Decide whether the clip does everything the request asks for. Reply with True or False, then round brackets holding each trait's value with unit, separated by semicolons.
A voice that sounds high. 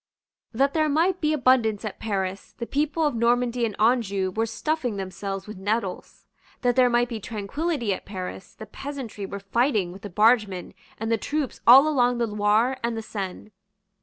True (230 Hz)